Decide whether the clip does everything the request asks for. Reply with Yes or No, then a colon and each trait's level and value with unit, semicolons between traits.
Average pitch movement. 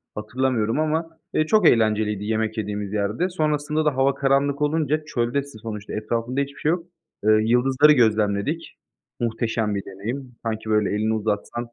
Yes: average, 4.9 semitones